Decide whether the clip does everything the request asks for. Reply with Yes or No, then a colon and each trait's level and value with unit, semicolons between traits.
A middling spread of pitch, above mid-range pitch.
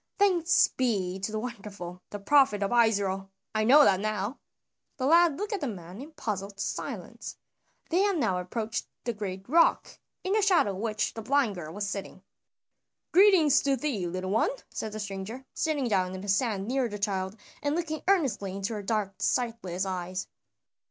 No: wide, 6.4 semitones; high, 215 Hz